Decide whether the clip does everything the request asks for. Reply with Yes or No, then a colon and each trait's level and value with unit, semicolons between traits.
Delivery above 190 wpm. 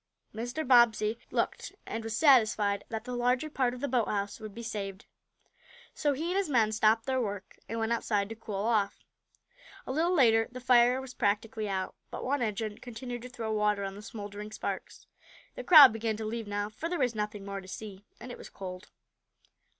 Yes: average, 200 wpm